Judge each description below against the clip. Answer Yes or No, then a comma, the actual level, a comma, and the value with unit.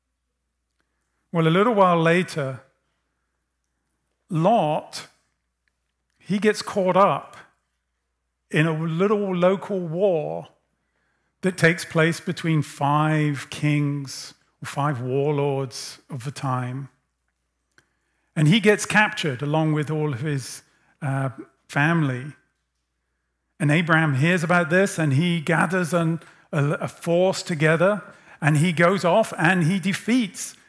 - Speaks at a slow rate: Yes, slow, 115 wpm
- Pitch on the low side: No, medium, 155 Hz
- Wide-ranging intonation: Yes, wide, 5.8 semitones